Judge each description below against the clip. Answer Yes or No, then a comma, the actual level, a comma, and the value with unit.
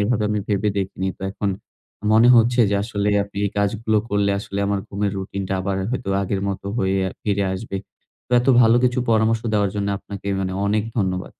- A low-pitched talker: Yes, low, 100 Hz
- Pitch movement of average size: No, narrow, 2.0 semitones